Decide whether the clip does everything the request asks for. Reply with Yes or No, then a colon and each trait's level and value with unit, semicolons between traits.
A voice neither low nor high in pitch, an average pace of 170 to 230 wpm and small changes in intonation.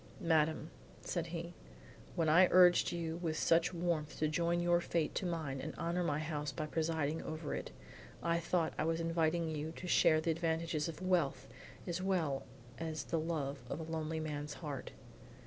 Yes: medium, 160 Hz; average, 180 wpm; narrow, 1.7 semitones